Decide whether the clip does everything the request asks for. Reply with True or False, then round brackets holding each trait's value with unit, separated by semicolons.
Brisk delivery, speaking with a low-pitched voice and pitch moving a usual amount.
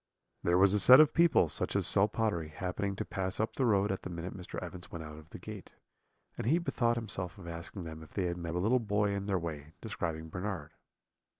True (235 wpm; 95 Hz; 3.7 semitones)